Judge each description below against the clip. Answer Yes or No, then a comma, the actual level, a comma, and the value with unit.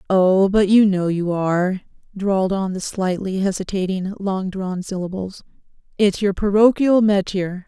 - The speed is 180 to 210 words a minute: No, average, 140 wpm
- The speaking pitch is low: No, high, 190 Hz